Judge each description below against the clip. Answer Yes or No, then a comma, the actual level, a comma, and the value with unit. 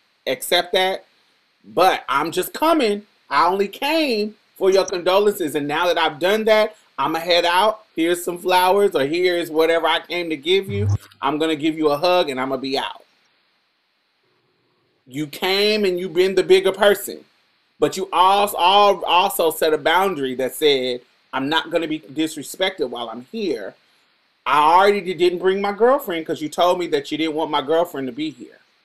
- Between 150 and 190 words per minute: Yes, average, 185 wpm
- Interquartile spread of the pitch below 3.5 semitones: No, average, 4.3 semitones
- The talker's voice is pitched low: No, medium, 180 Hz